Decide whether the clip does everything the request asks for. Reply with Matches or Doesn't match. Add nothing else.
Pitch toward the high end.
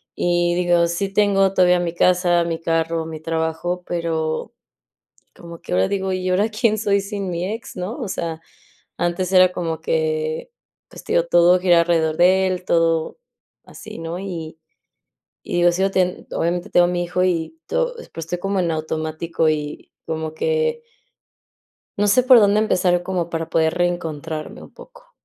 Doesn't match